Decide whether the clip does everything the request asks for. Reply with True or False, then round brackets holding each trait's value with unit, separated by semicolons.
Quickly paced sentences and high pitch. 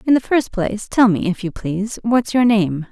True (245 wpm; 210 Hz)